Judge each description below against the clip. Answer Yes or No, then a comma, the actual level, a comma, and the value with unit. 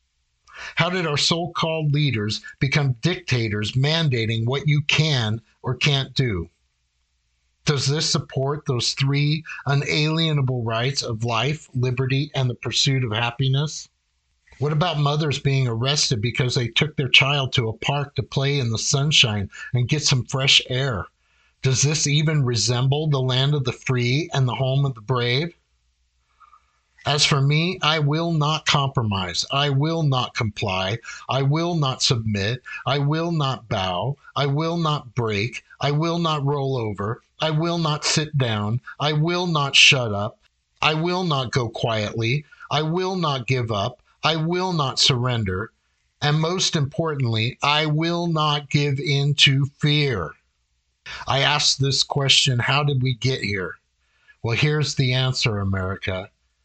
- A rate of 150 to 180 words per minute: Yes, average, 155 wpm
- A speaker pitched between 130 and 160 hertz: Yes, low, 135 Hz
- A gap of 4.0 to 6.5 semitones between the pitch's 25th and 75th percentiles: Yes, average, 4.3 semitones